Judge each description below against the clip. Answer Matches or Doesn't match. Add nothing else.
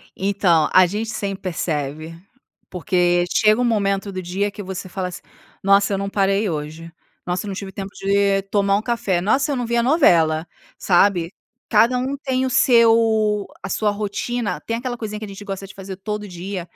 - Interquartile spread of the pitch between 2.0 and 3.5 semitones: Matches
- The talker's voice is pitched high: Matches